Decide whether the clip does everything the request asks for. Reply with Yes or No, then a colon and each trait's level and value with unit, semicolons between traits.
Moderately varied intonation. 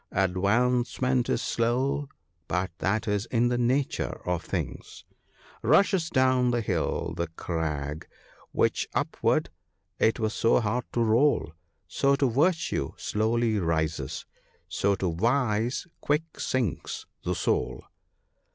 No: wide, 6.1 semitones